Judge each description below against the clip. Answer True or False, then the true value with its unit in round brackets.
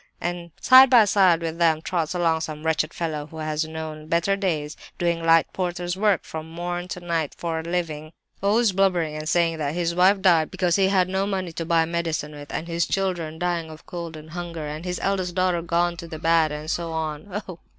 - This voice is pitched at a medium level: True (170 Hz)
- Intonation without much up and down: True (2.1 semitones)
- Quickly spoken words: True (215 wpm)